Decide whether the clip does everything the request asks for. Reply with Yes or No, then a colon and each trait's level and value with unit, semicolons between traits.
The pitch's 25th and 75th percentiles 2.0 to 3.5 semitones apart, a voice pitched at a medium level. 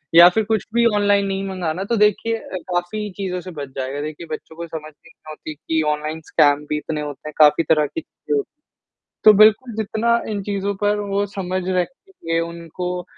No: average, 4.7 semitones; medium, 180 Hz